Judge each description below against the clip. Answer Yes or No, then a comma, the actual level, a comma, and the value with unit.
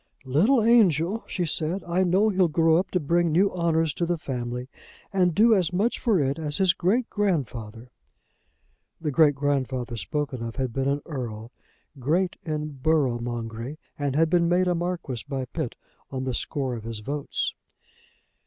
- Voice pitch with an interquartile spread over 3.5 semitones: Yes, wide, 5.4 semitones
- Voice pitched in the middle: Yes, medium, 155 Hz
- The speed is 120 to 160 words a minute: No, average, 170 wpm